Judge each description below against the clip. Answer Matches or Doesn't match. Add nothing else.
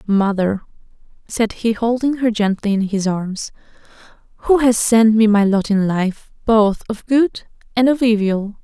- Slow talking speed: Doesn't match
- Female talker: Matches